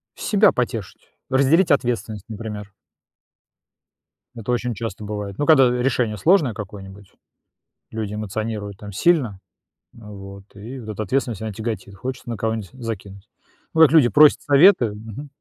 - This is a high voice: No, low, 110 Hz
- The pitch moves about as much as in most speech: Yes, average, 4.2 semitones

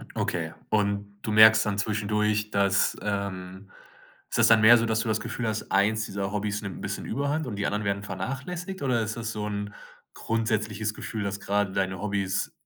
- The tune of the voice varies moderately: No, narrow, 1.7 semitones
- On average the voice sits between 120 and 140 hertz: No, low, 105 Hz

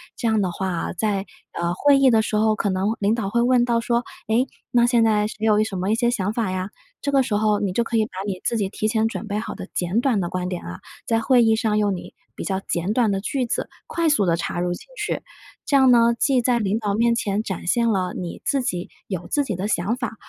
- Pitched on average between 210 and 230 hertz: Yes, high, 215 Hz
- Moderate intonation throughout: Yes, average, 3.6 semitones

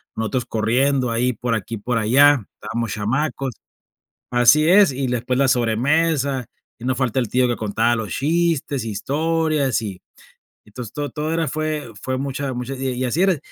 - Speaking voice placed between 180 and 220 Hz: No, low, 130 Hz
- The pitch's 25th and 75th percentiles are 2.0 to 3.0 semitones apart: No, average, 3.7 semitones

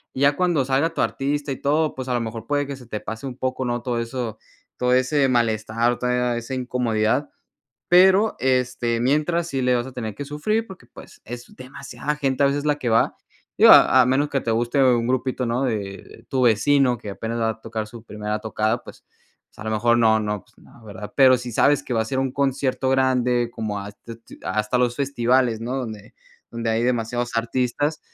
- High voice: No, low, 125 Hz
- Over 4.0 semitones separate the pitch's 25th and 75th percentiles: No, average, 2.9 semitones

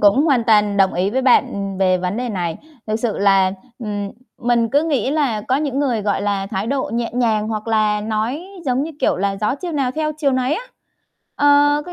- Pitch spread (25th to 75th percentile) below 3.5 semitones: No, average, 5.1 semitones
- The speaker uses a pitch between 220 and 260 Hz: Yes, high, 230 Hz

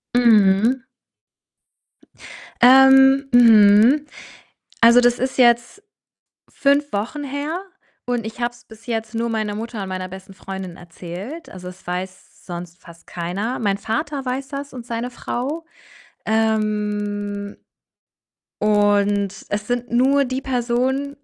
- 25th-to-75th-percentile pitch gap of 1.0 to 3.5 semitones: No, average, 4.2 semitones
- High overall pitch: Yes, high, 230 Hz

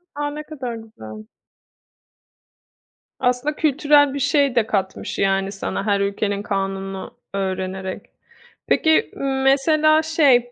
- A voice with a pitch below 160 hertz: No, high, 235 Hz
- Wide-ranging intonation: Yes, wide, 7.0 semitones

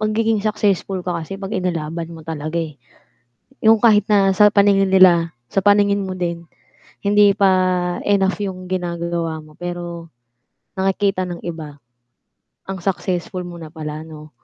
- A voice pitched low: No, medium, 185 Hz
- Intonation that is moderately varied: Yes, average, 3.0 semitones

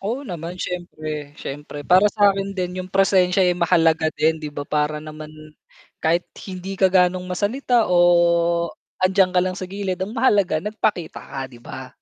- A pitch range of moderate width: Yes, average, 3.3 semitones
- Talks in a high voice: No, medium, 180 Hz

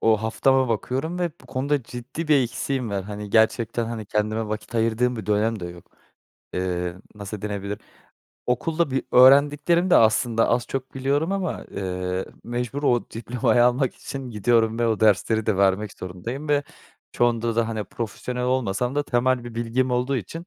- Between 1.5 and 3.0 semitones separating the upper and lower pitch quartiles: No, average, 3.5 semitones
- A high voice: No, low, 120 Hz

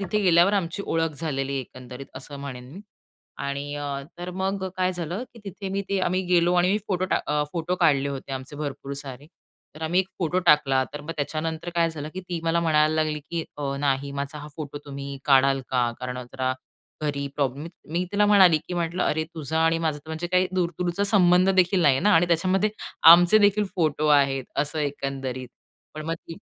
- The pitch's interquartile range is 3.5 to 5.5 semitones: Yes, average, 4.2 semitones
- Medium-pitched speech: Yes, medium, 160 Hz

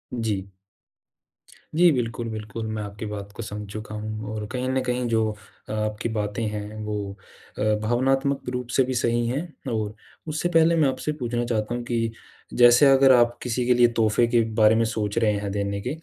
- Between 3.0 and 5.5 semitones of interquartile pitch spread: No, narrow, 2.6 semitones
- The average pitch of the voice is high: No, low, 115 Hz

